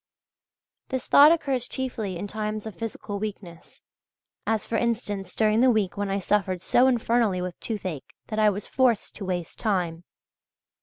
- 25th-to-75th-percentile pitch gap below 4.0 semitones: Yes, average, 3.5 semitones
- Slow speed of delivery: No, average, 160 wpm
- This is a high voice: Yes, high, 210 Hz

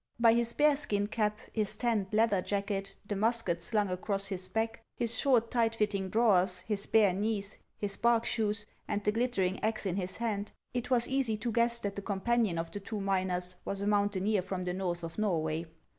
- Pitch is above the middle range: Yes, high, 205 Hz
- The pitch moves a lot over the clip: No, average, 3.0 semitones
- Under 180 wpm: No, average, 200 wpm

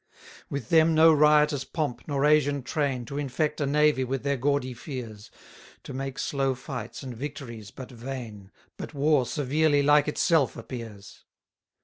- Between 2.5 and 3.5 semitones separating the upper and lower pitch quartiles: Yes, average, 3.1 semitones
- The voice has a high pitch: No, medium, 140 Hz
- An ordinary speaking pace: Yes, average, 155 wpm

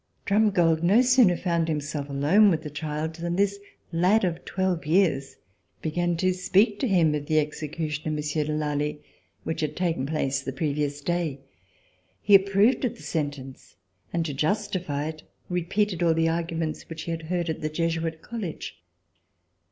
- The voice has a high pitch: No, medium, 165 Hz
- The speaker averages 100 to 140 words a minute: No, average, 165 wpm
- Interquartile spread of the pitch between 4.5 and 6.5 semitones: No, average, 3.3 semitones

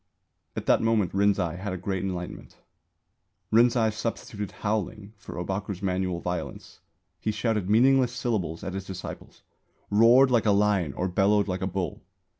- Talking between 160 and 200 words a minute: No, average, 150 wpm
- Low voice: Yes, low, 100 Hz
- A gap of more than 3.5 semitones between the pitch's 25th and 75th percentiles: No, average, 2.9 semitones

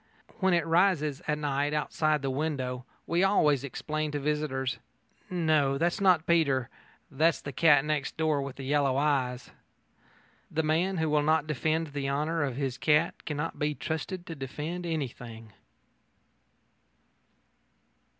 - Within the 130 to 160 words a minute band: Yes, average, 140 wpm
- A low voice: No, medium, 150 Hz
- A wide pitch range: No, average, 2.8 semitones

